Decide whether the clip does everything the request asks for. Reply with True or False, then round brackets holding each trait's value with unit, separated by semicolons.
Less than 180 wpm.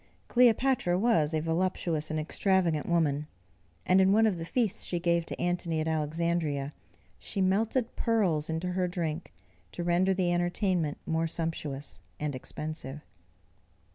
True (140 wpm)